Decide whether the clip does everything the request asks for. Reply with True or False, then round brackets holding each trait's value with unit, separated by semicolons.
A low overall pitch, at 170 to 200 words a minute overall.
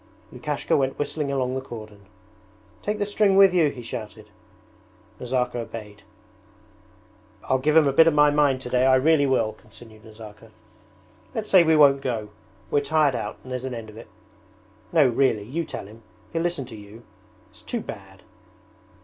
True (130 Hz; 175 wpm)